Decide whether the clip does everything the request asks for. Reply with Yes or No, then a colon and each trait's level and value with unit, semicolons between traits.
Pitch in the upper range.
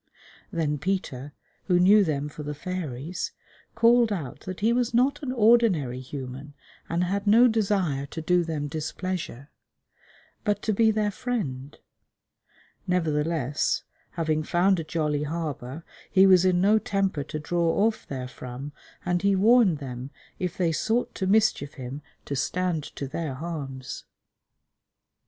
No: medium, 170 Hz